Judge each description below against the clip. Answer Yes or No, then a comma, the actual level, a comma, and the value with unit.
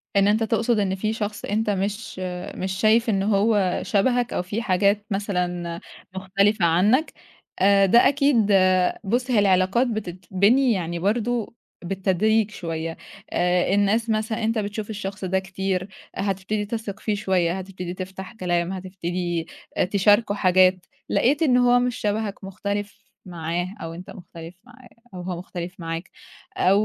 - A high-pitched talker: Yes, high, 195 Hz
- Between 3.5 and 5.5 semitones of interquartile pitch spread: No, average, 3.0 semitones